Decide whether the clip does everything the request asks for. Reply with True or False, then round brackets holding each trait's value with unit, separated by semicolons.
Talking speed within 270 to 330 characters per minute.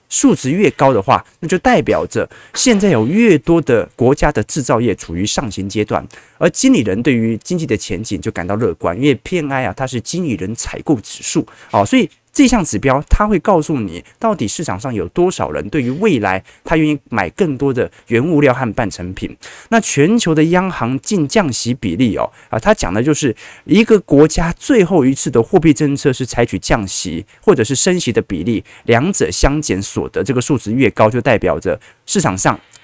True (300 characters per minute)